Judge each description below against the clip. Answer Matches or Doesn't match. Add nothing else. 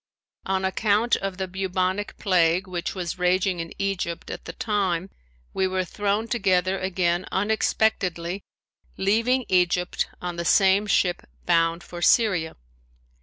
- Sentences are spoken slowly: Matches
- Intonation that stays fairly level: Matches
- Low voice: Doesn't match